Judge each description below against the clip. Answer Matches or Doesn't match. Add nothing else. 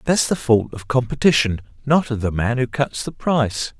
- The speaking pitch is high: Doesn't match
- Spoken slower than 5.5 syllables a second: Matches